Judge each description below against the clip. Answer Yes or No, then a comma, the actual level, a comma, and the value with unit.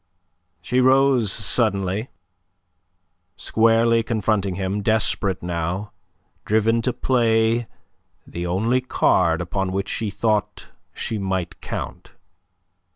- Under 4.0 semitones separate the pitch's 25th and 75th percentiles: Yes, average, 3.2 semitones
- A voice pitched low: Yes, low, 110 Hz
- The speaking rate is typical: No, slow, 95 wpm